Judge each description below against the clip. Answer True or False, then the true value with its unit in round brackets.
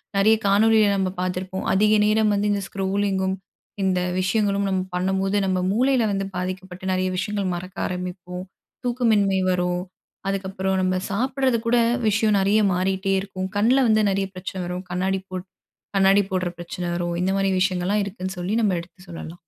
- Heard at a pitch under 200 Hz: True (190 Hz)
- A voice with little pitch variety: True (1.8 semitones)